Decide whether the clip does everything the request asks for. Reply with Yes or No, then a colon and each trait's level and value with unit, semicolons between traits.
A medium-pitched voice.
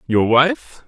Yes: medium, 145 Hz